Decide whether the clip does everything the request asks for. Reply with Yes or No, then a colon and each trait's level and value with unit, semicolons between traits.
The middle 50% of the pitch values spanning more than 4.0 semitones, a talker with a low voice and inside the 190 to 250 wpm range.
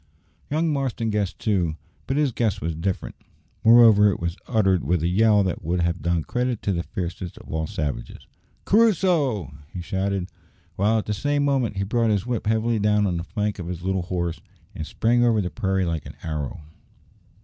Yes: average, 4.8 semitones; low, 100 Hz; average, 195 wpm